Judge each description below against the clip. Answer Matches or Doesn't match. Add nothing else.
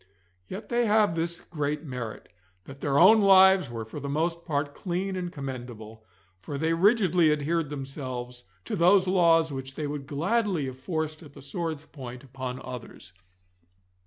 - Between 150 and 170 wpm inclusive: Matches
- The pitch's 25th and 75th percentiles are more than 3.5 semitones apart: Matches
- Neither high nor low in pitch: Matches